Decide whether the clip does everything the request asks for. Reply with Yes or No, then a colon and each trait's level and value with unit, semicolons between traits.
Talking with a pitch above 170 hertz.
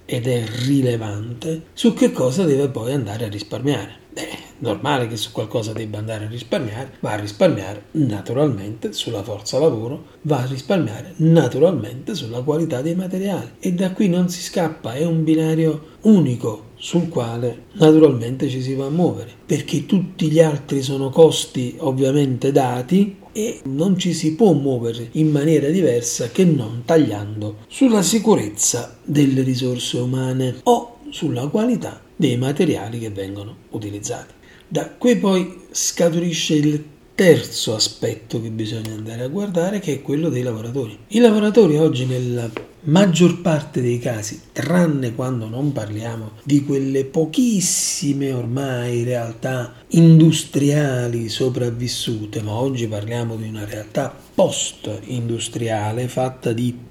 No: low, 135 Hz